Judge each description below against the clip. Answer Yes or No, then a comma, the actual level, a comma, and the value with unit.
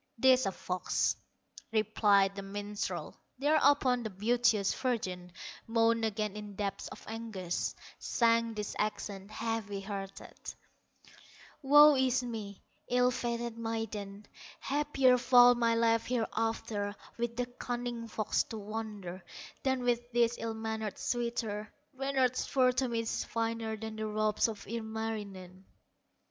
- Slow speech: Yes, slow, 125 wpm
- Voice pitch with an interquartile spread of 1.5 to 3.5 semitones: Yes, average, 2.7 semitones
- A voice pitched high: Yes, high, 225 Hz